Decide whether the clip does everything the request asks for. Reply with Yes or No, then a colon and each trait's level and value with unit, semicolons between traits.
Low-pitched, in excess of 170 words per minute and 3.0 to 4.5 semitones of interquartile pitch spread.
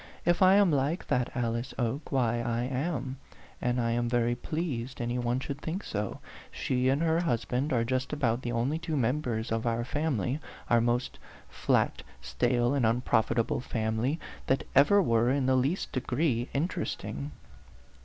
No: low, 125 Hz; average, 165 wpm; average, 3.4 semitones